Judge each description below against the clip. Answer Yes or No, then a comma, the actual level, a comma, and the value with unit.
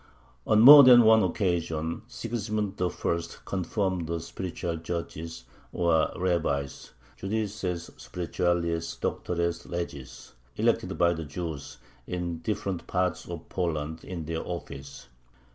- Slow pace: Yes, slow, 110 wpm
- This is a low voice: Yes, very low, 85 Hz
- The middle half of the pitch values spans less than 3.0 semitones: Yes, narrow, 2.5 semitones